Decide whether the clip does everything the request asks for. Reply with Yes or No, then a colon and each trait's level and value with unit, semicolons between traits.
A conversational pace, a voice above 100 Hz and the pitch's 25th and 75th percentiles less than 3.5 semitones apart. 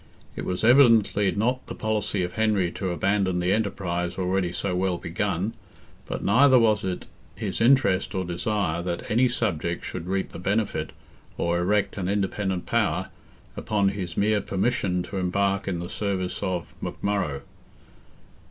No: average, 150 wpm; very low, 95 Hz; average, 2.8 semitones